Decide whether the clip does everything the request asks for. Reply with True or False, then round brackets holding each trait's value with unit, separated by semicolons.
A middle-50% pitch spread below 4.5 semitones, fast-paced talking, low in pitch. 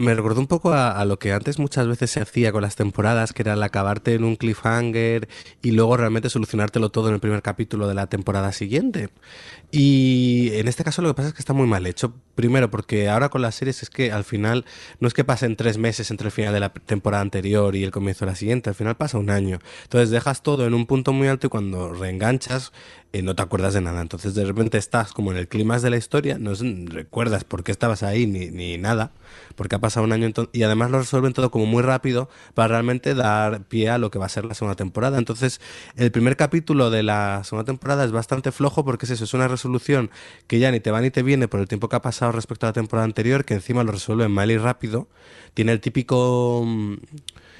True (3.2 semitones; 245 wpm; 115 Hz)